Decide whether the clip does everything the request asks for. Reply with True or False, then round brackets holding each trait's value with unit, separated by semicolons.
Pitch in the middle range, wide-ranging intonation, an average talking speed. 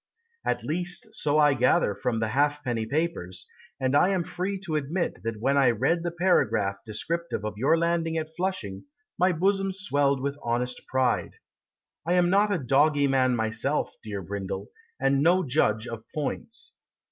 True (145 Hz; 6.2 semitones; 165 wpm)